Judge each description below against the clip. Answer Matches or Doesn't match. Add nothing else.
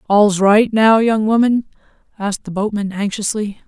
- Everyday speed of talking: Matches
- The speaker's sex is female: Matches